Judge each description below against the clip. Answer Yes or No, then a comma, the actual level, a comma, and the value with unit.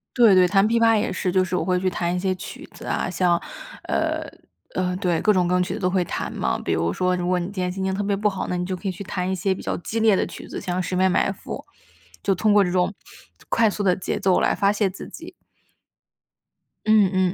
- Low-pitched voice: No, medium, 185 Hz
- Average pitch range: No, narrow, 1.7 semitones